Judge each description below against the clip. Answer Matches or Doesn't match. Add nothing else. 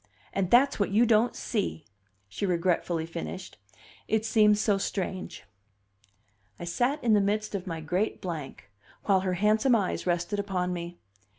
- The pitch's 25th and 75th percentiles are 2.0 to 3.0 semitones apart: Doesn't match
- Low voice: Doesn't match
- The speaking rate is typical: Matches